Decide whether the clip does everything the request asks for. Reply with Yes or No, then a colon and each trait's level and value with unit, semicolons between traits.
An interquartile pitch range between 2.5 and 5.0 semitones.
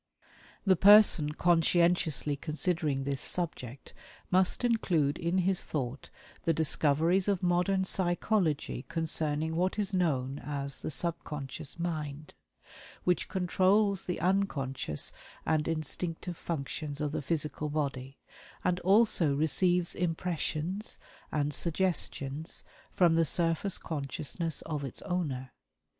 Yes: average, 3.6 semitones